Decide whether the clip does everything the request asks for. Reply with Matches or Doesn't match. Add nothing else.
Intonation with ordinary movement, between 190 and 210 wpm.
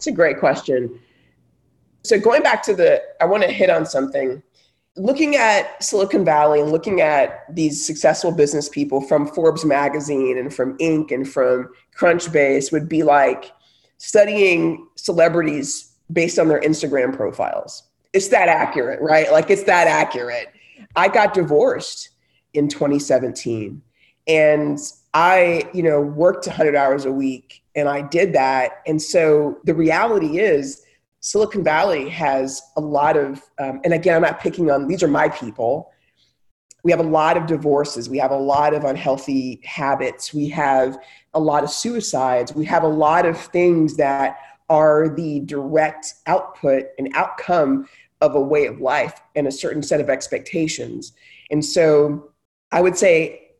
Doesn't match